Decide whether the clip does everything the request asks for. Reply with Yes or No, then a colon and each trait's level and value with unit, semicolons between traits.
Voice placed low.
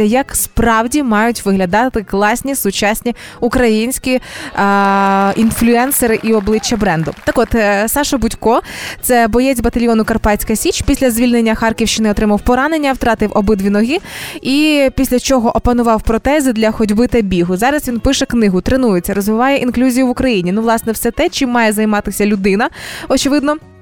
No: high, 230 Hz